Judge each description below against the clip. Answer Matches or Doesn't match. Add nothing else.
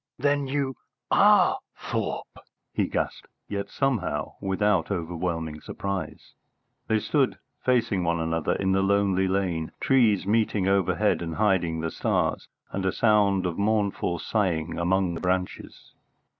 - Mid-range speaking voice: Doesn't match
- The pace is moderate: Doesn't match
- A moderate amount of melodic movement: Matches